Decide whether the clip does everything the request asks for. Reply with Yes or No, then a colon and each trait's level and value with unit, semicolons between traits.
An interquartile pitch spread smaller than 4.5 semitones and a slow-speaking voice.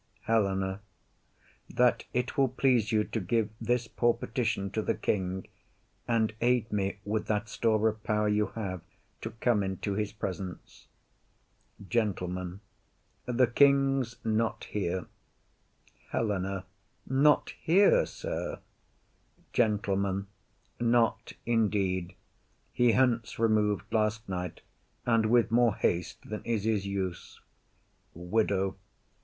Yes: average, 3.3 semitones; slow, 115 wpm